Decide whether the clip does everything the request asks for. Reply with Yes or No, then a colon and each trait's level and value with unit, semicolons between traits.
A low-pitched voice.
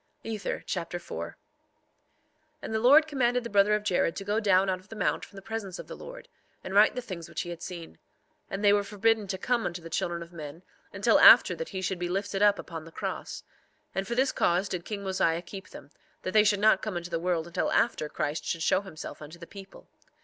No: high, 195 Hz